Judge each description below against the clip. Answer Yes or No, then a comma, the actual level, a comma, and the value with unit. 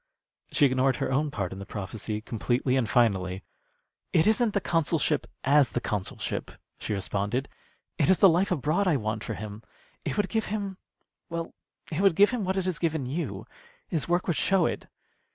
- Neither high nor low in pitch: Yes, medium, 145 Hz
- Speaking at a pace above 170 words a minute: Yes, average, 190 wpm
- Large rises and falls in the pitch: Yes, wide, 8.2 semitones